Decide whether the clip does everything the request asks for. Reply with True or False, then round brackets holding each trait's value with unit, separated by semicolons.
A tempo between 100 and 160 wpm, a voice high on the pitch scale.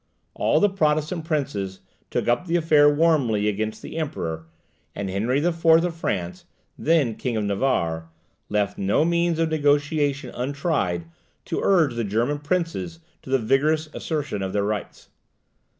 False (150 wpm; 145 Hz)